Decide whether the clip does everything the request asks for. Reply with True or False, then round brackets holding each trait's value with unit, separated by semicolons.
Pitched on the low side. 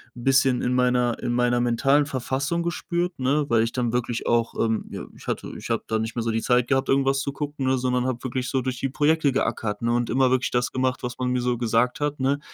True (125 Hz)